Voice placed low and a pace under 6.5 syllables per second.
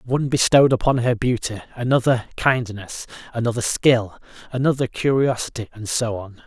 Yes: low, 120 Hz; 5.3 syllables/s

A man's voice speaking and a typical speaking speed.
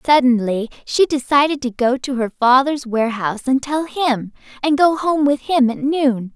No: female; average, 180 wpm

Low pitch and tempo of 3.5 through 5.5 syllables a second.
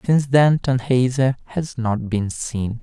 Yes: low, 125 Hz; 4.5 syllables/s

